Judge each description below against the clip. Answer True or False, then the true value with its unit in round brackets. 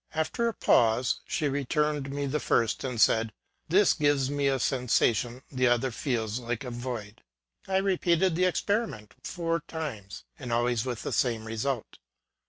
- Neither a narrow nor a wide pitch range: True (4.7 semitones)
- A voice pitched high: False (130 Hz)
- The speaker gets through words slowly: False (165 wpm)